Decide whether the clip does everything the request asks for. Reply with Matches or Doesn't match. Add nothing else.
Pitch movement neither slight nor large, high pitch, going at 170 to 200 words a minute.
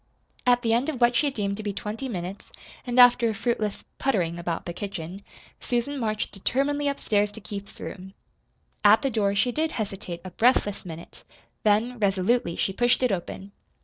Matches